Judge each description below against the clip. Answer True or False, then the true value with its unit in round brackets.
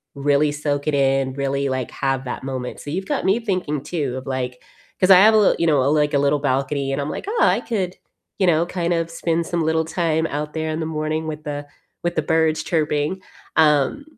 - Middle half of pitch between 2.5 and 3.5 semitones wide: True (3.1 semitones)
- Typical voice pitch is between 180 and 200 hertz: False (150 Hz)